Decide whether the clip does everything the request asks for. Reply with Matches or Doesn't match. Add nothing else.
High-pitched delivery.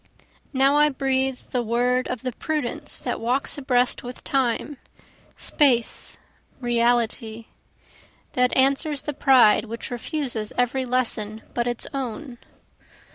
Matches